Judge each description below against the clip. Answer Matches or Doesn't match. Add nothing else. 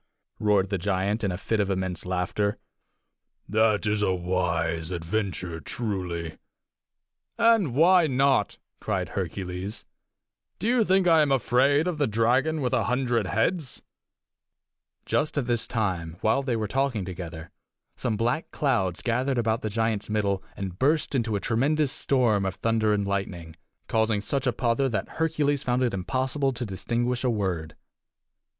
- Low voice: Matches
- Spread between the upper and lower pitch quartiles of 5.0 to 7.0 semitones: Matches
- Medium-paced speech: Matches